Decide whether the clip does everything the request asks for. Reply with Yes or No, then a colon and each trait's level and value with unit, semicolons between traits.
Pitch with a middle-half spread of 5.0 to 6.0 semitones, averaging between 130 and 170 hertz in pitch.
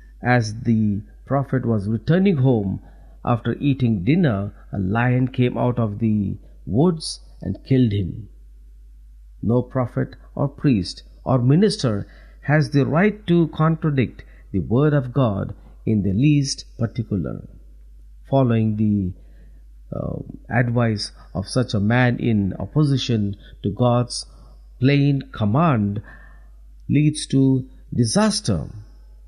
No: wide, 5.5 semitones; low, 115 Hz